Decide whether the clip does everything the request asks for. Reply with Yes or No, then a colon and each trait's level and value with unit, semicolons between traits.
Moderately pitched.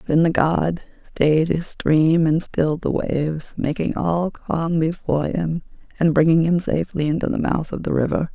Yes: medium, 160 Hz